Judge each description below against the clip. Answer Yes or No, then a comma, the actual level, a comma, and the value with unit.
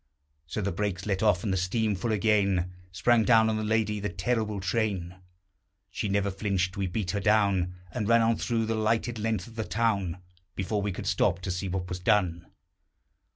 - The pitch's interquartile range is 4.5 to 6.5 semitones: No, average, 3.1 semitones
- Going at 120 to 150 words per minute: No, average, 200 wpm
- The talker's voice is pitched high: No, low, 100 Hz